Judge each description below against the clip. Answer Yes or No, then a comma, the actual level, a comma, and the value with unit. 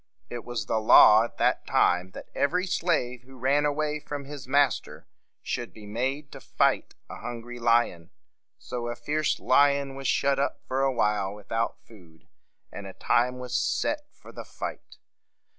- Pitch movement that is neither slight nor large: Yes, average, 3.6 semitones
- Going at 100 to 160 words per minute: No, average, 170 wpm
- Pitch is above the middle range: No, low, 125 Hz